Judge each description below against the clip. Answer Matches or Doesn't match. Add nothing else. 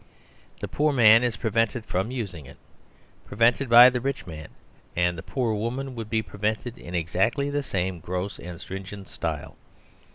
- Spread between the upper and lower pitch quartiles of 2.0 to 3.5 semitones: Doesn't match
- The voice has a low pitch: Matches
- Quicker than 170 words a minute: Doesn't match